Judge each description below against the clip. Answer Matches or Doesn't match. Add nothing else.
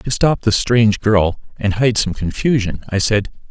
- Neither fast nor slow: Matches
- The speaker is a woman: Doesn't match